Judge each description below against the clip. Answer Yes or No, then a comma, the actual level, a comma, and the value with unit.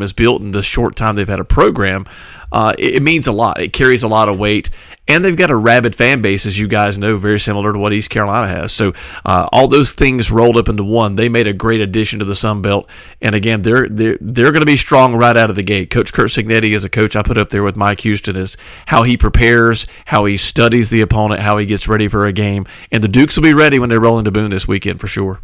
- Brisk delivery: Yes, fast, 275 wpm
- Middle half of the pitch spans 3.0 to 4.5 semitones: No, narrow, 2.4 semitones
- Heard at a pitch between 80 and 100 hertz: No, low, 110 Hz